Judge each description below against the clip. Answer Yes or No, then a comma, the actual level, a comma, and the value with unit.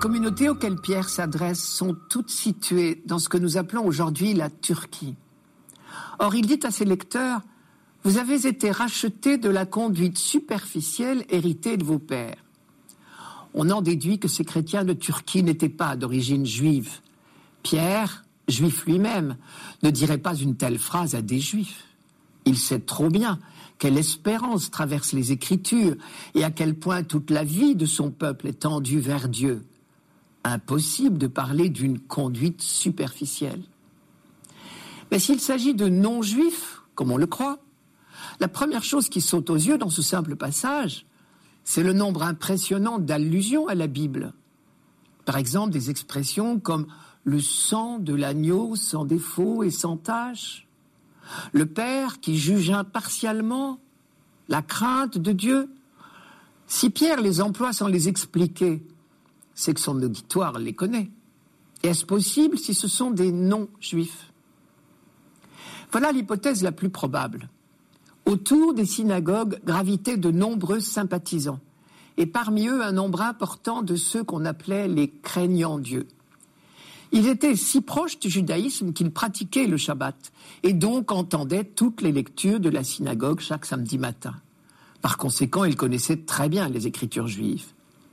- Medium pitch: Yes, medium, 180 Hz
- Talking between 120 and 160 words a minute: Yes, slow, 145 wpm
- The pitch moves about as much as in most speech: No, wide, 5.9 semitones